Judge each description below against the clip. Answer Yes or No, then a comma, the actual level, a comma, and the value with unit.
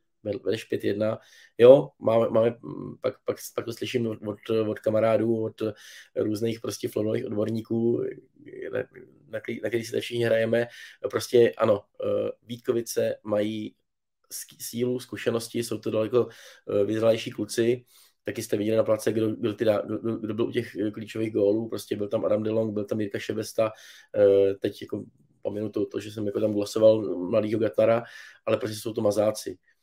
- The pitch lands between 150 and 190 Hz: No, low, 110 Hz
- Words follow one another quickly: No, average, 155 wpm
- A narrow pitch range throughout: Yes, narrow, 1.7 semitones